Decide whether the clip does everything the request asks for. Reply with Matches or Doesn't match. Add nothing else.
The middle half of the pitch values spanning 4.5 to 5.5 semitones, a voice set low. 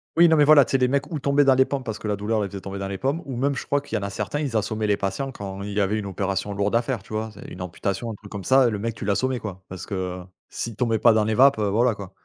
Matches